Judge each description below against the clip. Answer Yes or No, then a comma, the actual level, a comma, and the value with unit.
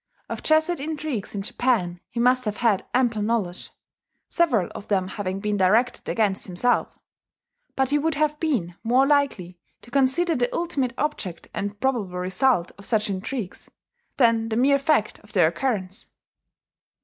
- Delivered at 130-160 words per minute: Yes, average, 155 wpm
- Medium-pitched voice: No, high, 230 Hz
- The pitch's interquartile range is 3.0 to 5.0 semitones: No, wide, 5.6 semitones